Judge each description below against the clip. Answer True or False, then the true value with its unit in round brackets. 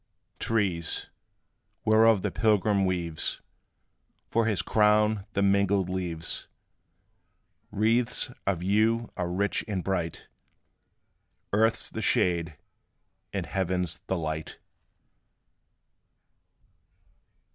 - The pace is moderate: False (90 wpm)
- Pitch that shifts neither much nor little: True (3.4 semitones)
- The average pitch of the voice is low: True (100 Hz)